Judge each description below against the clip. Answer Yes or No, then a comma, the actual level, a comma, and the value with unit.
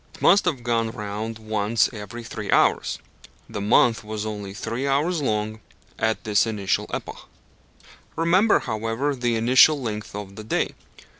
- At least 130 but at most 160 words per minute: Yes, average, 150 wpm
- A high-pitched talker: No, low, 110 Hz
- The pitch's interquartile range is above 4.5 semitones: No, average, 2.8 semitones